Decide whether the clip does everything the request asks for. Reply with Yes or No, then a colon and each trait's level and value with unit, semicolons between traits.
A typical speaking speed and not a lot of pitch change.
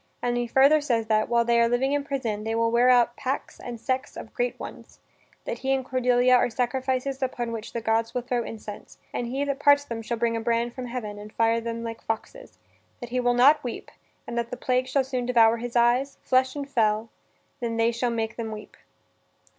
No: fast, 225 wpm; narrow, 2.1 semitones